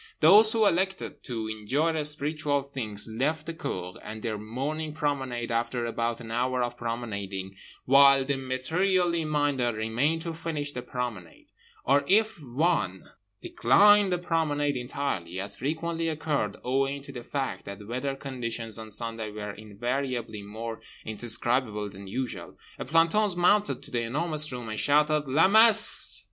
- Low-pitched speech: Yes, low, 130 Hz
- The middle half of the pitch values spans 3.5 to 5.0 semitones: No, wide, 5.4 semitones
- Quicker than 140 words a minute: Yes, average, 150 wpm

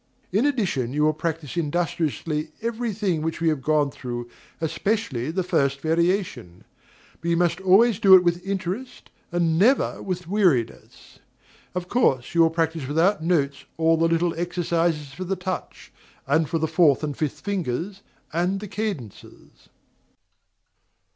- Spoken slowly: No, average, 150 wpm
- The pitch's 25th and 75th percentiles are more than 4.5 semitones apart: No, average, 3.5 semitones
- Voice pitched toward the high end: No, medium, 170 Hz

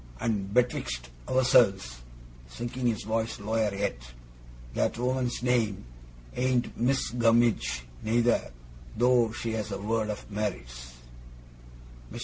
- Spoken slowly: Yes, slow, 115 wpm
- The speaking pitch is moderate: No, low, 110 Hz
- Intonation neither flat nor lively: Yes, average, 3.5 semitones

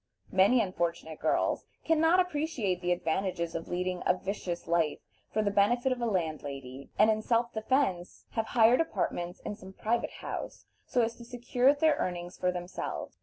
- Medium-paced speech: Yes, average, 170 wpm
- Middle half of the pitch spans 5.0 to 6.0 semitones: Yes, wide, 5.6 semitones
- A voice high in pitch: Yes, high, 200 Hz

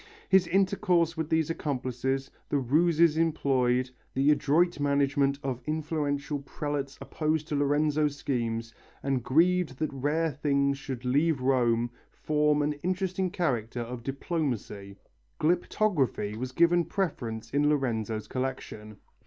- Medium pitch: Yes, medium, 145 Hz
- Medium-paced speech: No, slow, 120 wpm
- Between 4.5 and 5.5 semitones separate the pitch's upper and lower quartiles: No, average, 3.9 semitones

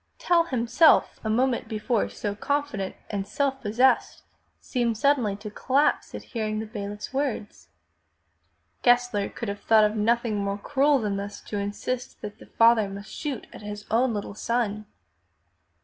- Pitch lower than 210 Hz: No, high, 220 Hz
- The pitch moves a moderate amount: Yes, average, 3.5 semitones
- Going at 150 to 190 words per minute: Yes, average, 155 wpm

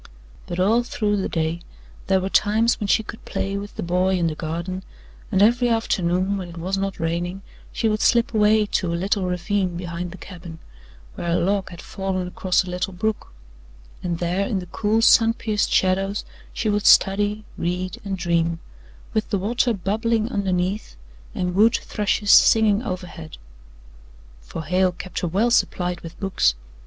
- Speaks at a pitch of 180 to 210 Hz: Yes, high, 190 Hz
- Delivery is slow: No, average, 175 wpm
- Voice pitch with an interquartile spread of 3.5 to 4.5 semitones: No, average, 2.9 semitones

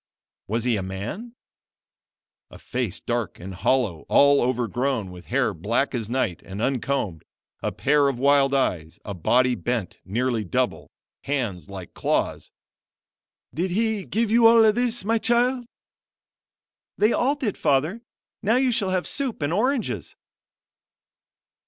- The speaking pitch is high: No, low, 135 Hz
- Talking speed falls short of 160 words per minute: Yes, average, 140 wpm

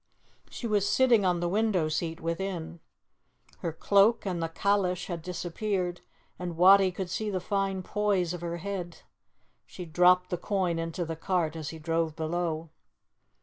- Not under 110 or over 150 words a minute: No, average, 160 wpm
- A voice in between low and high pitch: Yes, medium, 180 Hz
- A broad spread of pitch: No, average, 2.9 semitones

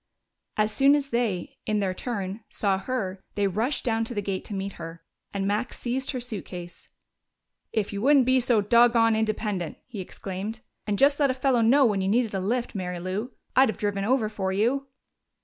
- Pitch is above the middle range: Yes, high, 215 Hz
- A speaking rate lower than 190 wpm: No, average, 200 wpm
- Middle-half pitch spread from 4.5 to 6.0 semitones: No, average, 4.0 semitones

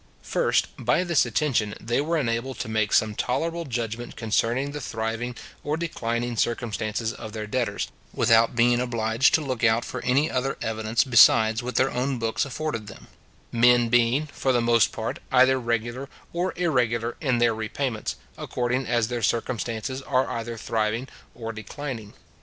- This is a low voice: Yes, low, 120 Hz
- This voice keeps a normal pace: Yes, average, 160 wpm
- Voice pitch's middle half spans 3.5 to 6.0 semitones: No, narrow, 2.5 semitones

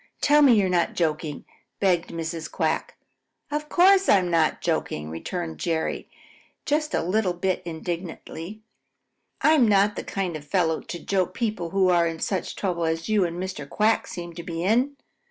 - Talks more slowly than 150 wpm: No, average, 175 wpm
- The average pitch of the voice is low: No, medium, 180 Hz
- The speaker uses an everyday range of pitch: Yes, average, 4.1 semitones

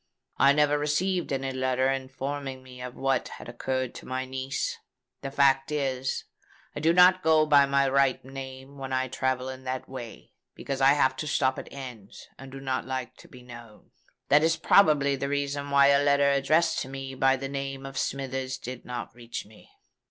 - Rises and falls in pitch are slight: Yes, narrow, 1.4 semitones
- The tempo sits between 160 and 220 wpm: Yes, average, 195 wpm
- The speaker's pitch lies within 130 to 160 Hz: Yes, low, 135 Hz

